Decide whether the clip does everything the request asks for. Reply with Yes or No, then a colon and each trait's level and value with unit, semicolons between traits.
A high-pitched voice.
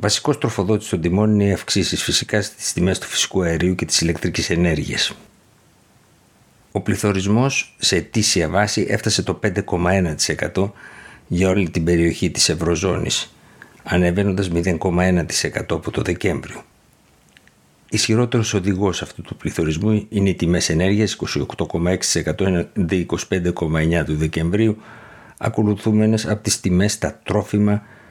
No: very low, 95 Hz